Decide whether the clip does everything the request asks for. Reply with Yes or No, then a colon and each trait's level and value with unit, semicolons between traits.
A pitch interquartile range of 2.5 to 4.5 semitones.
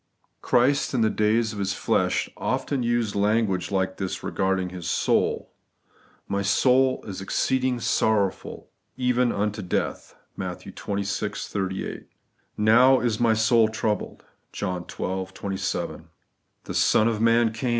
Yes: average, 3.4 semitones